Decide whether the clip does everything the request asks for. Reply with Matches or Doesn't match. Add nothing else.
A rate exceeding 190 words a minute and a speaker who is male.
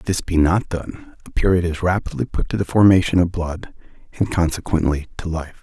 Matches